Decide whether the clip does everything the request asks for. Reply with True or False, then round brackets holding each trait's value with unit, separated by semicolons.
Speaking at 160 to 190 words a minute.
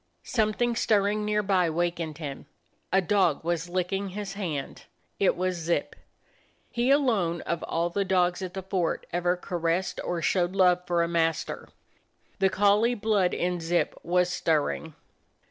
False (150 wpm)